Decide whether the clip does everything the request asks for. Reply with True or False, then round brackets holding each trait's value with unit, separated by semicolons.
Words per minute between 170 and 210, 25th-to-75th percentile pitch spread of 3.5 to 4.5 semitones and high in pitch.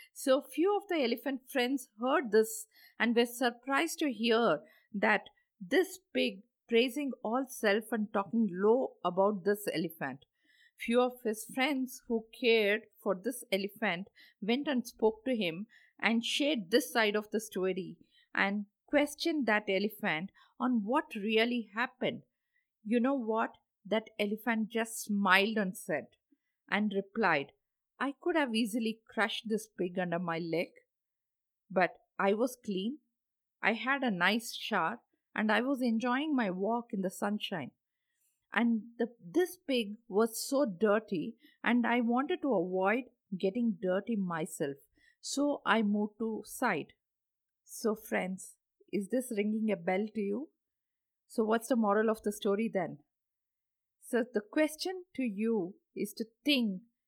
False (145 wpm; 4.0 semitones; 230 Hz)